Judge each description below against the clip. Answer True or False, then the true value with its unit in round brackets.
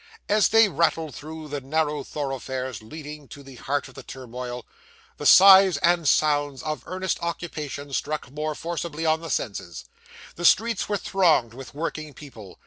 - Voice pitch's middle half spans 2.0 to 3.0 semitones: False (3.8 semitones)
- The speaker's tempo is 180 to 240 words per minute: False (160 wpm)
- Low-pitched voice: False (150 Hz)